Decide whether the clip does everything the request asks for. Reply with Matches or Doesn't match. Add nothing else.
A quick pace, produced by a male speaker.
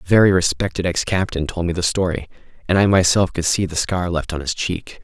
Matches